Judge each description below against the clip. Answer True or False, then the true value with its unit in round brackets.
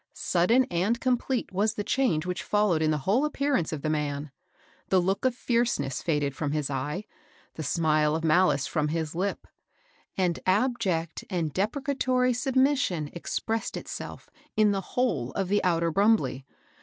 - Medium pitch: True (180 Hz)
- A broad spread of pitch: True (6.8 semitones)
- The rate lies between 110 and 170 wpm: True (160 wpm)